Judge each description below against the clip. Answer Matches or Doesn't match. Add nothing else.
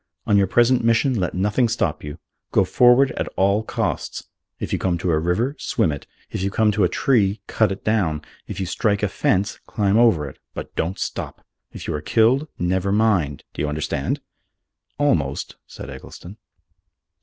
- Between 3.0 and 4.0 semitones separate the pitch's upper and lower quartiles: Doesn't match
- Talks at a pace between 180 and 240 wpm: Matches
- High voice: Doesn't match